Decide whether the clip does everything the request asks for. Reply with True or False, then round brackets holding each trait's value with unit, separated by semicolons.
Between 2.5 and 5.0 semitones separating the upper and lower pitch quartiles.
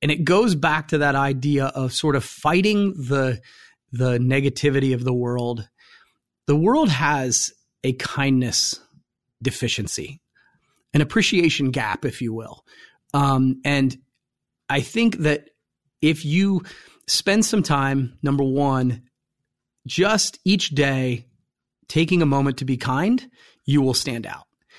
True (3.3 semitones)